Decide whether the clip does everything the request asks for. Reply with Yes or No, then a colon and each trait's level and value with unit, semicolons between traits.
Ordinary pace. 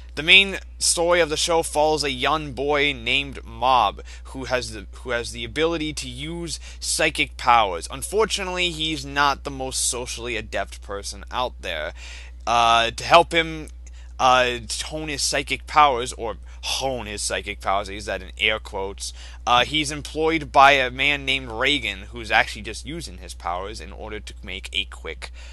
Yes: average, 170 wpm